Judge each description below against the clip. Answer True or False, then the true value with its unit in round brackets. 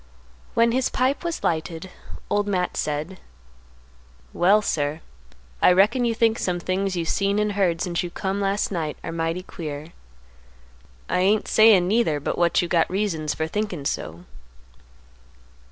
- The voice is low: False (185 Hz)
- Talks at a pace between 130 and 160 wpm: True (155 wpm)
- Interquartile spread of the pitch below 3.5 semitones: False (4.0 semitones)